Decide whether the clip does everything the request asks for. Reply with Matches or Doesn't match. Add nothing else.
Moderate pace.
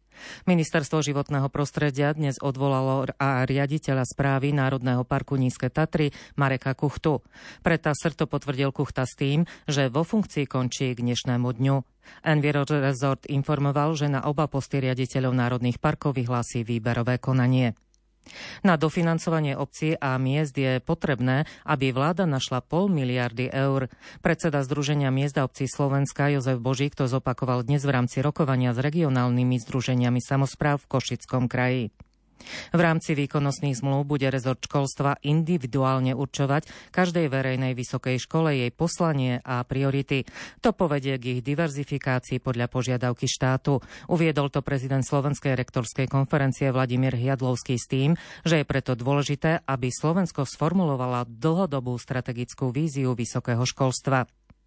Matches